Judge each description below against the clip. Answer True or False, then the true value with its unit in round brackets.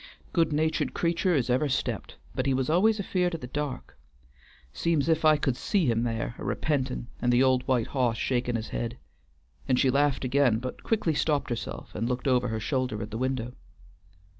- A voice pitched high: False (130 Hz)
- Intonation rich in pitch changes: False (4.0 semitones)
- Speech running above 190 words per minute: True (200 wpm)